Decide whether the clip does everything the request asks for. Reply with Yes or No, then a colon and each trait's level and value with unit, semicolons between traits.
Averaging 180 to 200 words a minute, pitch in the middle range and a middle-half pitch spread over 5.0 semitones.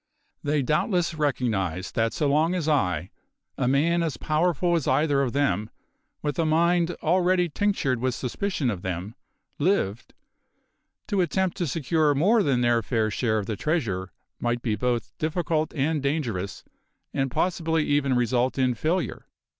No: average, 155 wpm; medium, 145 Hz; wide, 5.6 semitones